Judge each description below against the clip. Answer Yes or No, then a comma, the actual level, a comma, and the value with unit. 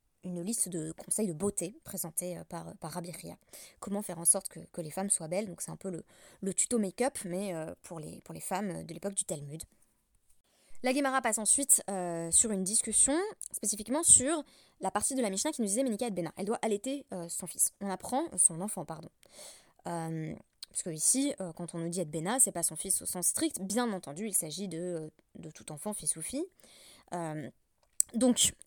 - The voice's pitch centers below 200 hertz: Yes, high, 190 Hz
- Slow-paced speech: No, average, 215 wpm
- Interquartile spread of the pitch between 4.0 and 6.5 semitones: Yes, average, 4.7 semitones